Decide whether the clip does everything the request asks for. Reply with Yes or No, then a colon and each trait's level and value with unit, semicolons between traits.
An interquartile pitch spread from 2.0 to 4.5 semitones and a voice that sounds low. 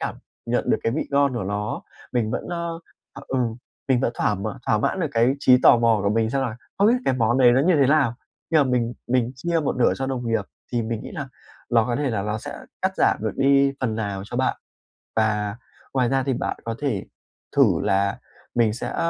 Yes: average, 3.4 semitones; low, 120 Hz